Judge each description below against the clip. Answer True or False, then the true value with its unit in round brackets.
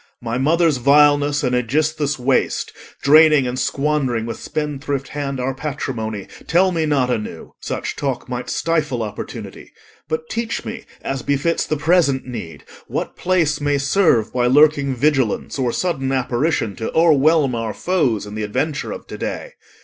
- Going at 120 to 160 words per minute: True (155 wpm)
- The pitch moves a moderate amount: True (3.8 semitones)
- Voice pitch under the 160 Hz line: True (140 Hz)